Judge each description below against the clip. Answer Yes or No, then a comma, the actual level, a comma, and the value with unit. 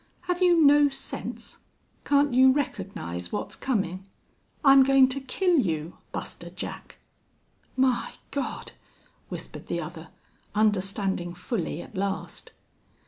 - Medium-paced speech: No, slow, 115 wpm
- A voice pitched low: No, very high, 250 Hz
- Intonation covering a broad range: Yes, wide, 6.5 semitones